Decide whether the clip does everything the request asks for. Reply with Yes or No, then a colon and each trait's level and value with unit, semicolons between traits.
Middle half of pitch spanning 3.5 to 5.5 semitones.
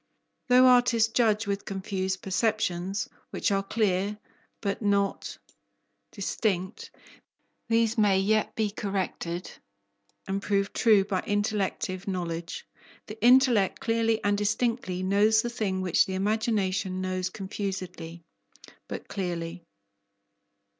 No: average, 2.7 semitones